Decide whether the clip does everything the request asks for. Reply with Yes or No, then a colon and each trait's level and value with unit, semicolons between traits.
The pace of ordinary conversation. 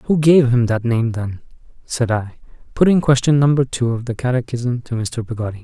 Yes: average, 190 wpm